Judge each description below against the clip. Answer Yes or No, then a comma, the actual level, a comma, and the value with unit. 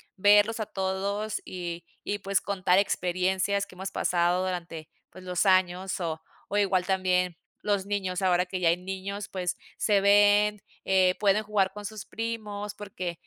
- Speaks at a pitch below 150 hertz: No, high, 190 Hz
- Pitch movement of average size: No, narrow, 2.0 semitones